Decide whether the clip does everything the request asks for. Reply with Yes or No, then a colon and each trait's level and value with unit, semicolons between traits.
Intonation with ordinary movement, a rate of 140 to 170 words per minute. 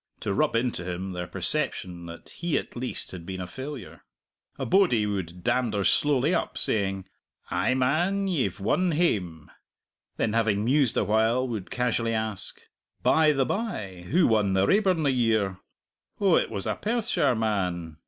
No: wide, 7.4 semitones; average, 160 wpm